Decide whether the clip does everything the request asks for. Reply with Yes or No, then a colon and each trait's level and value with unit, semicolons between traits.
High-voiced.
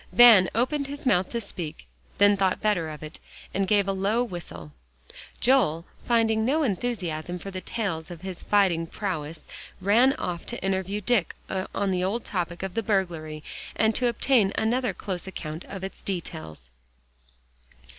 Yes: high, 195 Hz